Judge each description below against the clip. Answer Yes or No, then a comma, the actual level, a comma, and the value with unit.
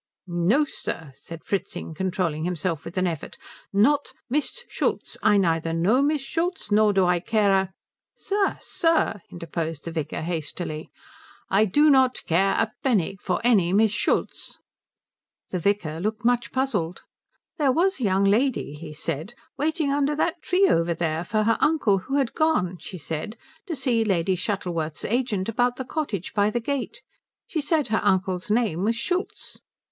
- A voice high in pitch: Yes, high, 205 Hz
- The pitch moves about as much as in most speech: No, wide, 7.2 semitones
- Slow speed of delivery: No, average, 165 wpm